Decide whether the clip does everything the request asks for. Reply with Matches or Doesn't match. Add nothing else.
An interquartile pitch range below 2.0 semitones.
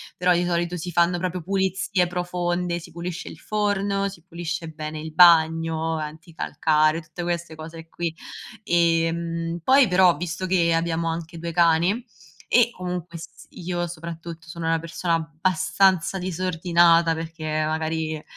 Matches